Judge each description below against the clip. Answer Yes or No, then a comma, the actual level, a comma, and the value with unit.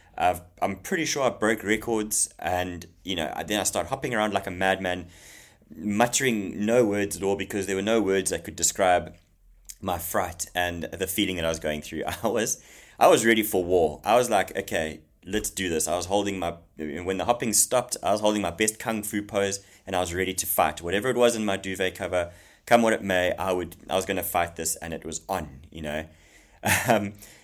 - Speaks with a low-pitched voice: Yes, very low, 95 Hz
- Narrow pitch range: No, average, 3.2 semitones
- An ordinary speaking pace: No, fast, 225 wpm